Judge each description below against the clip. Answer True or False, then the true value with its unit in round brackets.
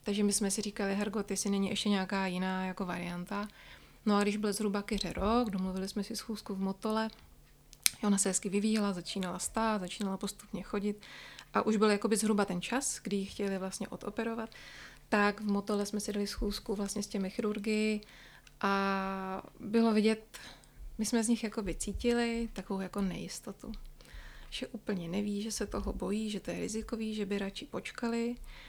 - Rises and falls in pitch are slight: True (1.8 semitones)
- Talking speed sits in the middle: False (175 wpm)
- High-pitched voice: True (205 Hz)